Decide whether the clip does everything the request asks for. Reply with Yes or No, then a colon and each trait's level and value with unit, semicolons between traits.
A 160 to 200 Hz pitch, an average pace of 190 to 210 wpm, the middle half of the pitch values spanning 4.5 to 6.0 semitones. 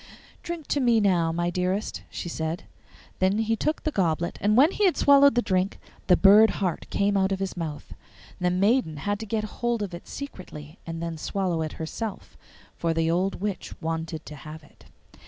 Yes: high, 190 Hz; average, 195 wpm; average, 4.8 semitones